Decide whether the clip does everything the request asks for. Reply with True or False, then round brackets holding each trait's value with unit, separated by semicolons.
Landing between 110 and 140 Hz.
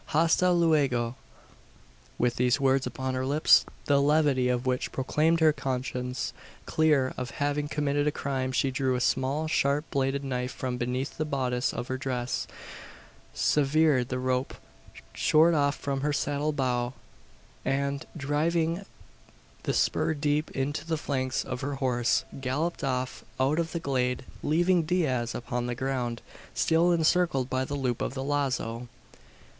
True (135 Hz)